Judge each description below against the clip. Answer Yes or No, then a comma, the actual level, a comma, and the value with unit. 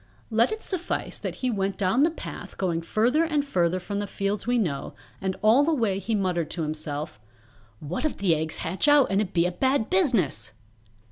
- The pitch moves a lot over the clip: Yes, wide, 6.8 semitones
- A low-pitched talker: No, high, 195 Hz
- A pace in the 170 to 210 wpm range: Yes, fast, 205 wpm